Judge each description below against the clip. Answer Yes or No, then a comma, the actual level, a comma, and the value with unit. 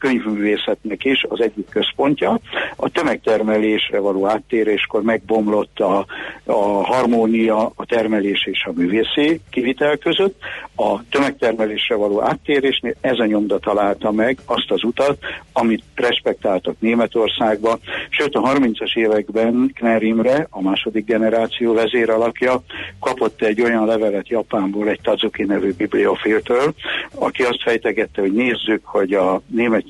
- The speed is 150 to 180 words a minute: No, average, 125 wpm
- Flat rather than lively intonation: Yes, narrow, 1.7 semitones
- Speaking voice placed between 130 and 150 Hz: No, low, 110 Hz